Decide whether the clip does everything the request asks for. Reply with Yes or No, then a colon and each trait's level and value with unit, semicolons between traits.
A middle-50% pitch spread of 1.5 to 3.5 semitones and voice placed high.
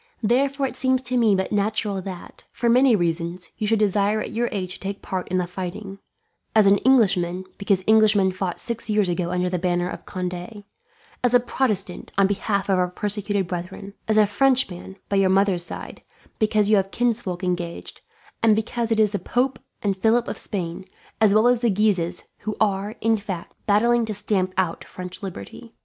Yes: average, 3.1 semitones; high, 200 Hz